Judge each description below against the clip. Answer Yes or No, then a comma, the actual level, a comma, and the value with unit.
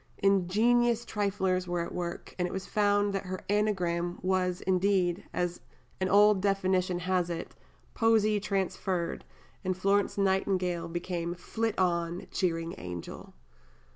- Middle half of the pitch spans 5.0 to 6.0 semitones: No, narrow, 2.4 semitones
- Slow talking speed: Yes, slow, 130 wpm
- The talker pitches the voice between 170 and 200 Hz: Yes, medium, 185 Hz